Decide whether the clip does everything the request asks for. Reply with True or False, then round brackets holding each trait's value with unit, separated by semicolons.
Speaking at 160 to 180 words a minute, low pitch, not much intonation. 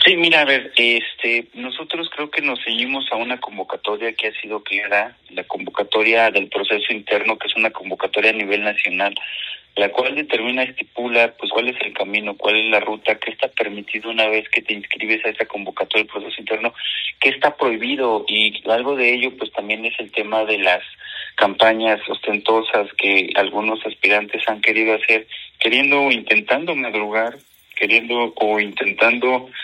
True (170 wpm; 110 Hz; 2.2 semitones)